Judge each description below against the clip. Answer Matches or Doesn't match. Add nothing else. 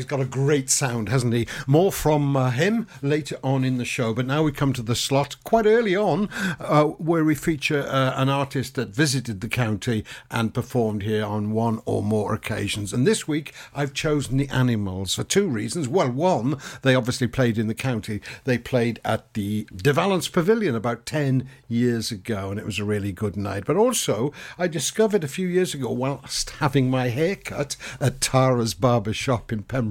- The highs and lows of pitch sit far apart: Doesn't match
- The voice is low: Matches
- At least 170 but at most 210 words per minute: Matches